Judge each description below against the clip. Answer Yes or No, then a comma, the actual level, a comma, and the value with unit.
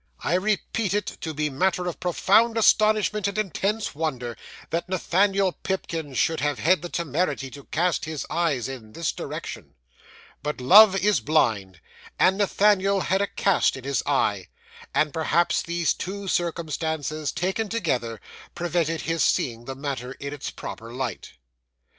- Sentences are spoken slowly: No, average, 150 wpm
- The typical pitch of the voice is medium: Yes, medium, 165 Hz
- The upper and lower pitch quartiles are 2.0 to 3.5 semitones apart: No, average, 5.3 semitones